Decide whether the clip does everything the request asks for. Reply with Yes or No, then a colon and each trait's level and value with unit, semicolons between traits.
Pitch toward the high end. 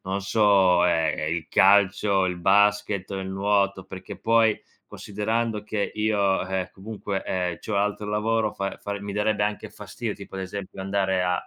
No: low, 100 Hz